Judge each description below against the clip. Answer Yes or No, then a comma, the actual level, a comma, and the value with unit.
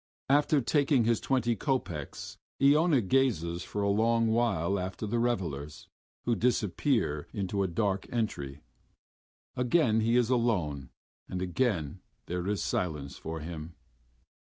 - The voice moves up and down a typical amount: No, wide, 6.0 semitones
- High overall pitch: No, low, 105 Hz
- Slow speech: Yes, slow, 130 wpm